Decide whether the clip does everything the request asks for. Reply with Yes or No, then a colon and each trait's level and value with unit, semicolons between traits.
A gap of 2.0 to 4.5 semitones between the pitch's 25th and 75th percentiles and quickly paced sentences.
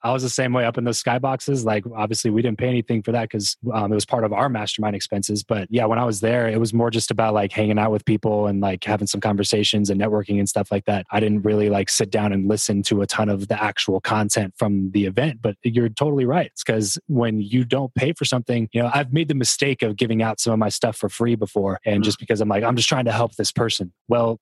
Yes: narrow, 2.5 semitones; fast, 275 wpm